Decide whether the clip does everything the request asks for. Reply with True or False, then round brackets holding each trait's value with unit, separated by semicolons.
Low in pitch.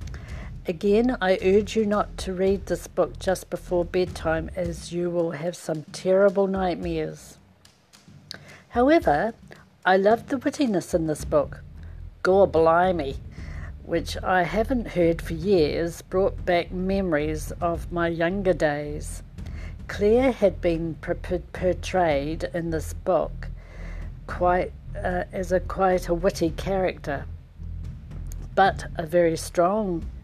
False (175 Hz)